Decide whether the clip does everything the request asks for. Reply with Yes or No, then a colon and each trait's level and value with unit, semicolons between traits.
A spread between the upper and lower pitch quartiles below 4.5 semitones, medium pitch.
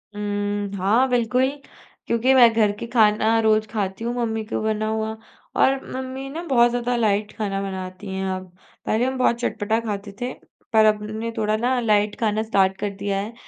No: narrow, 2.5 semitones; high, 220 Hz